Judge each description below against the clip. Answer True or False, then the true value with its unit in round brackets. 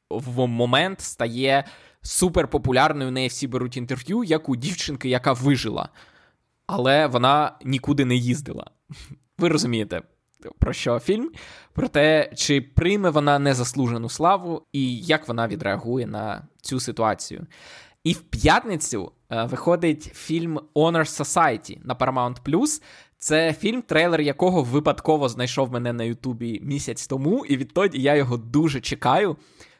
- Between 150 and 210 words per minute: False (130 wpm)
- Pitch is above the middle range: False (140 Hz)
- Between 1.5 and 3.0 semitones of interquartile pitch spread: False (3.9 semitones)